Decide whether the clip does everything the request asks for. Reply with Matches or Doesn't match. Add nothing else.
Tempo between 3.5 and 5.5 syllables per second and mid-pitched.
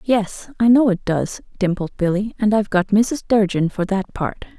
Doesn't match